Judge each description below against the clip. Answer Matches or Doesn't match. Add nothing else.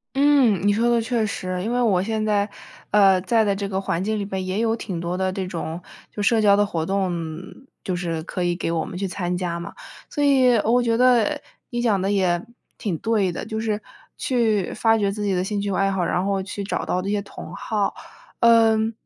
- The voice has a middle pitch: Doesn't match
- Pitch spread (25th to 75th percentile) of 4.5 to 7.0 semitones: Doesn't match